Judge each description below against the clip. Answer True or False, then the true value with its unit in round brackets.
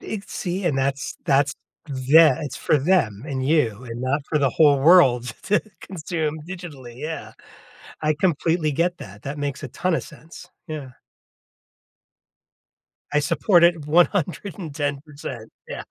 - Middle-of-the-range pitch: True (150 Hz)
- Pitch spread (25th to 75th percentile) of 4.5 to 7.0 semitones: False (3.7 semitones)